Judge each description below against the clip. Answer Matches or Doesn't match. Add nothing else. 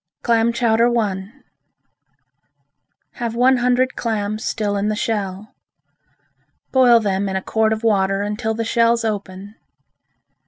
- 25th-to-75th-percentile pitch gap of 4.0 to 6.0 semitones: Doesn't match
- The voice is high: Matches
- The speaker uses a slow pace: Matches